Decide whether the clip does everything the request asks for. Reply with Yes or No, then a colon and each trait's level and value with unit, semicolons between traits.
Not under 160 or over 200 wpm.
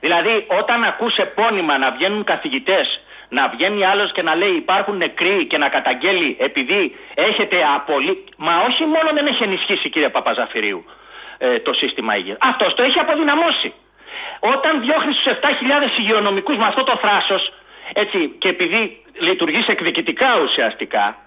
No: average, 145 wpm